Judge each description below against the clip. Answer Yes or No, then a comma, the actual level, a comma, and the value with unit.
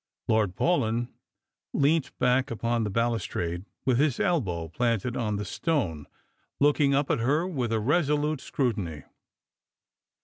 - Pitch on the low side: Yes, low, 120 Hz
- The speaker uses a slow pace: Yes, slow, 125 wpm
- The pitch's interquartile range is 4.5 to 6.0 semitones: Yes, average, 5.3 semitones